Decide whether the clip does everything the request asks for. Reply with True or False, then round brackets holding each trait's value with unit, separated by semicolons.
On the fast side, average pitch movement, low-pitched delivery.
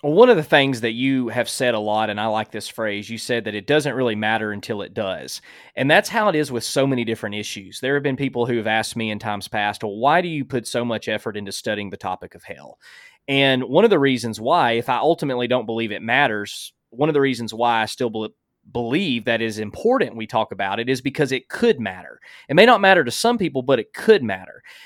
True (255 wpm; 4.6 semitones; 120 Hz)